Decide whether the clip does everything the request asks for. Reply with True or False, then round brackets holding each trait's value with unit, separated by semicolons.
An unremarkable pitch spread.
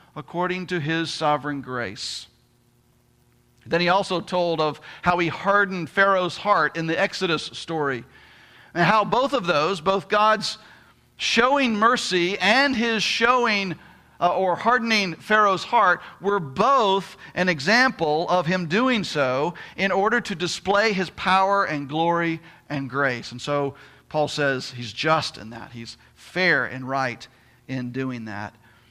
False (6.2 semitones)